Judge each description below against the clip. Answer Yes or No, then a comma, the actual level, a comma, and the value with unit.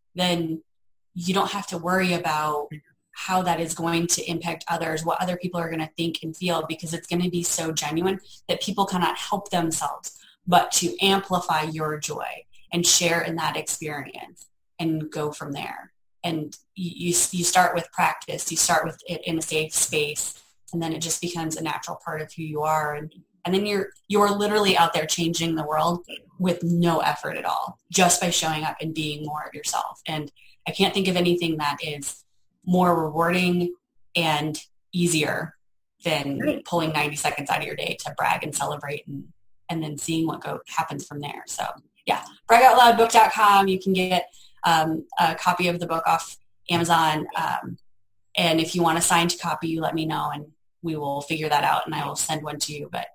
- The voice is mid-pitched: Yes, medium, 165 Hz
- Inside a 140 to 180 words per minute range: No, average, 200 wpm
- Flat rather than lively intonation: Yes, narrow, 2.3 semitones